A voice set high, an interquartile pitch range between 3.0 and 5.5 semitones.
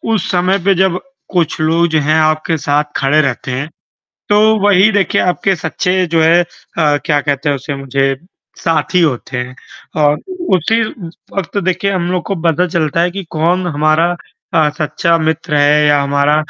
No: medium, 160 Hz; average, 3.6 semitones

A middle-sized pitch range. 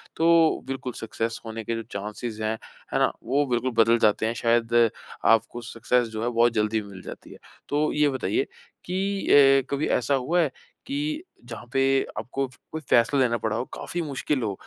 Yes: average, 4.2 semitones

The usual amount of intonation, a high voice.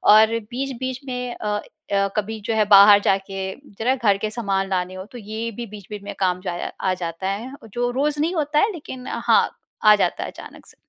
Yes: average, 4.0 semitones; high, 220 Hz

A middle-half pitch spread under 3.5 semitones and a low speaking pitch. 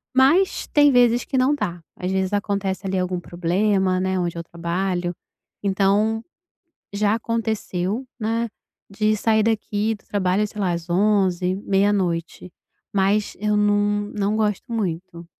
No: average, 2.7 semitones; high, 200 Hz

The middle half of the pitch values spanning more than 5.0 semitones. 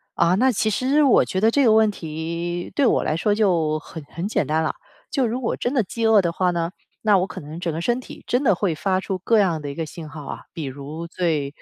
Yes: wide, 5.5 semitones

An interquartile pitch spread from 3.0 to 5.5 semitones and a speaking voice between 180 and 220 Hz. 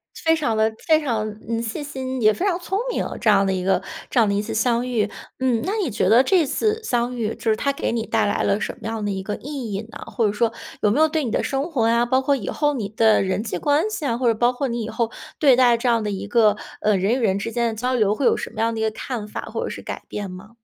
No: average, 3.8 semitones; high, 230 Hz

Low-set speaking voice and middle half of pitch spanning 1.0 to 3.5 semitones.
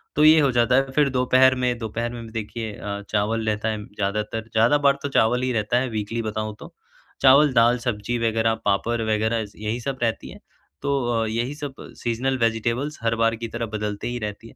Yes: low, 115 Hz; narrow, 2.6 semitones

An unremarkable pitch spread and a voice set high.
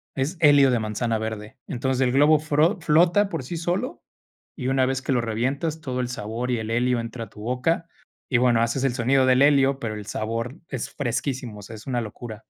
No: average, 3.5 semitones; low, 125 Hz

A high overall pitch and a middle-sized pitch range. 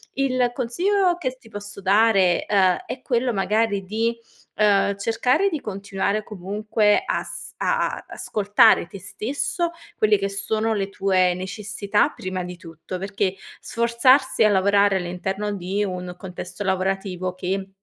Yes: high, 200 Hz; average, 3.0 semitones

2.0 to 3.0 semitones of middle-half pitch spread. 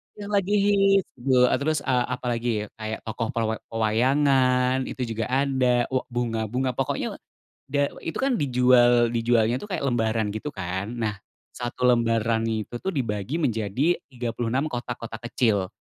Yes: average, 2.7 semitones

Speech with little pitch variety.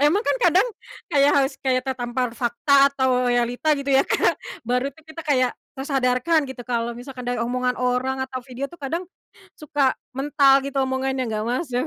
Yes: narrow, 2.0 semitones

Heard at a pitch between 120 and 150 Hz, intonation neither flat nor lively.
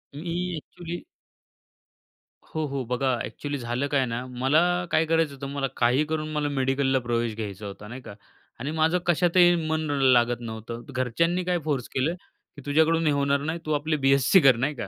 Yes: medium, 140 Hz; average, 4.2 semitones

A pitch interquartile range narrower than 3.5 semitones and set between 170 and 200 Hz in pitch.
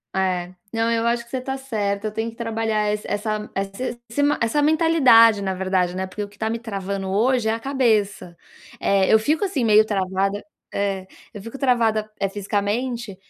No: average, 3.0 semitones; high, 215 Hz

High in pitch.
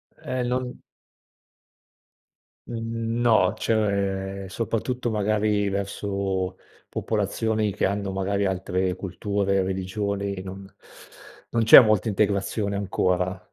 No: low, 100 Hz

